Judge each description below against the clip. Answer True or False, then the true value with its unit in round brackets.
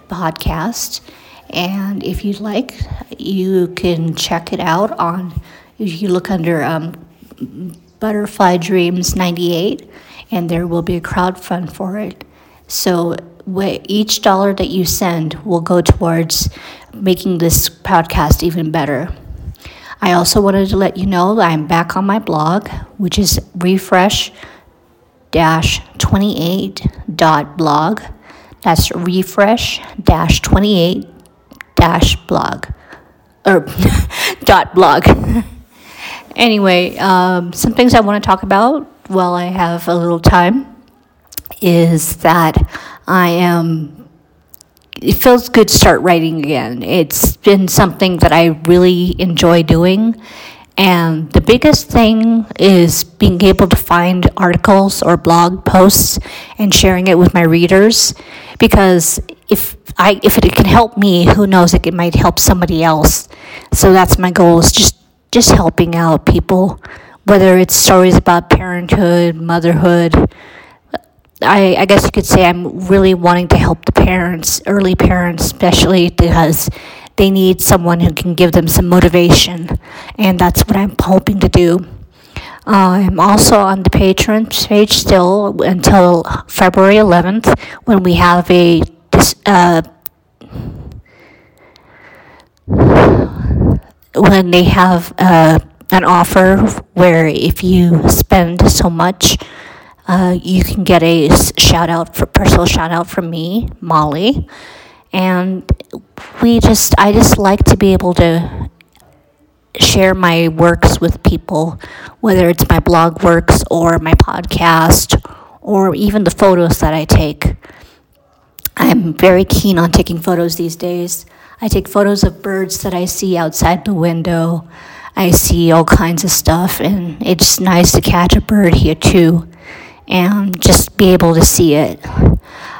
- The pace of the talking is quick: False (135 wpm)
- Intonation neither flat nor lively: False (2.3 semitones)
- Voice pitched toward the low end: False (180 Hz)